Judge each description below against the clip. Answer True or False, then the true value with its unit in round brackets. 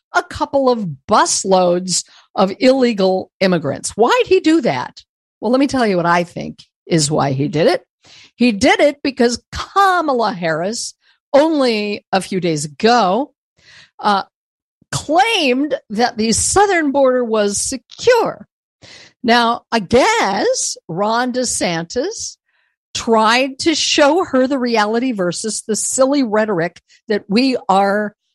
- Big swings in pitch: True (5.7 semitones)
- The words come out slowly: True (130 wpm)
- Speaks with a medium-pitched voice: False (240 Hz)